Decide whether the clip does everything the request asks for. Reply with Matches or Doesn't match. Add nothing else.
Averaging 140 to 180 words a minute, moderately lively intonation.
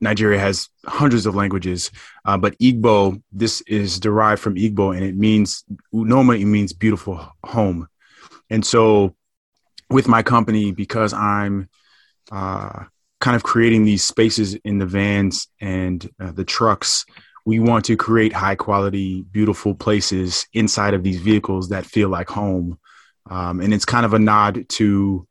Doesn't match